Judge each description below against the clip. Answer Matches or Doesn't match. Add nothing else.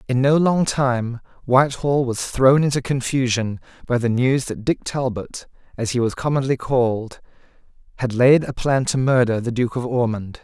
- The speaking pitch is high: Doesn't match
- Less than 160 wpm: Doesn't match